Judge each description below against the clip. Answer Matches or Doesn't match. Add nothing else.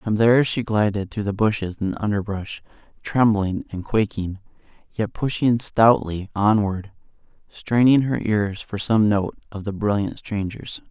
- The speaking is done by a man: Matches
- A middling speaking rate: Matches